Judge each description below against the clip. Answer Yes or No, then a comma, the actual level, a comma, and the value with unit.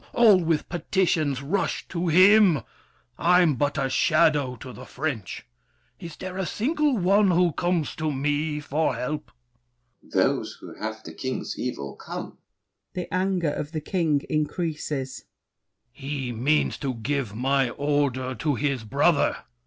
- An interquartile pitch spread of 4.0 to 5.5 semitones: Yes, average, 4.6 semitones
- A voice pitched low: No, medium, 150 Hz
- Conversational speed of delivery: Yes, average, 155 wpm